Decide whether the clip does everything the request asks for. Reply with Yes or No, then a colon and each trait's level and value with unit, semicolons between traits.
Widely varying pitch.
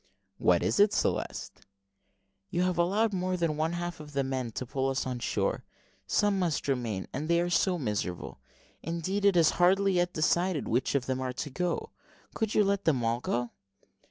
Yes: wide, 5.8 semitones